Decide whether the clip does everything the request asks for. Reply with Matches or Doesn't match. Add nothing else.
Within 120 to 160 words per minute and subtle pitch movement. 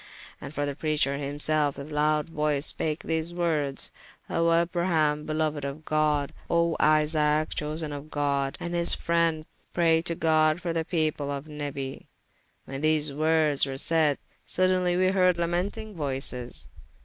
Matches